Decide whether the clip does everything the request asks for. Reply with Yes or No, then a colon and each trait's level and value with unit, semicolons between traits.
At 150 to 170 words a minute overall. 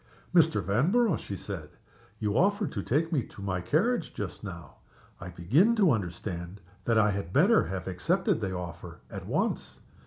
Yes: average, 165 wpm